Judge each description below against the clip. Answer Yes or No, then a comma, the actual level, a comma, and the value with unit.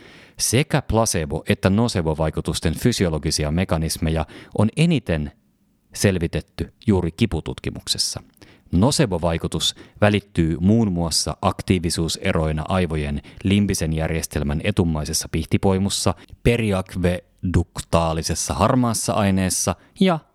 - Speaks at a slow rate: Yes, slow, 75 wpm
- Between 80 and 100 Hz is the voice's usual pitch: Yes, very low, 90 Hz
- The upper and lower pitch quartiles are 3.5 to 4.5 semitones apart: Yes, average, 4.1 semitones